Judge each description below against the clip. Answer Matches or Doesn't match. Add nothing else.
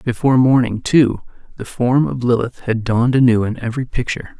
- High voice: Doesn't match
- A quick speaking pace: Doesn't match